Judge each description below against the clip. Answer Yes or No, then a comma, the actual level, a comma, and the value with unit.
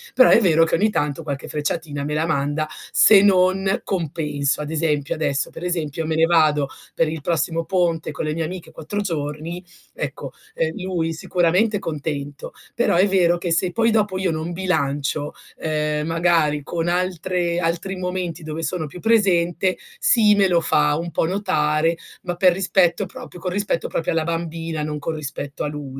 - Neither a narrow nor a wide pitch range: Yes, average, 3.2 semitones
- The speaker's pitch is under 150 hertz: No, medium, 165 Hz